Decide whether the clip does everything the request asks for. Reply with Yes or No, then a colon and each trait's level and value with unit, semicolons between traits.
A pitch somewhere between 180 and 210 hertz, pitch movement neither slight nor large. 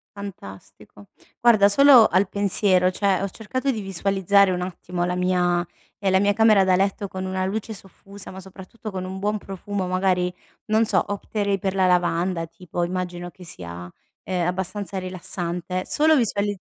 No: high, 190 Hz; narrow, 2.0 semitones